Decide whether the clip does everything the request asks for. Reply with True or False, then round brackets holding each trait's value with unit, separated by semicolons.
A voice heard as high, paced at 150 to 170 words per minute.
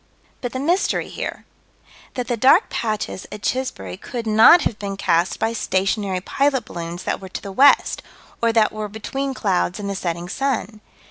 False (215 Hz; 180 wpm)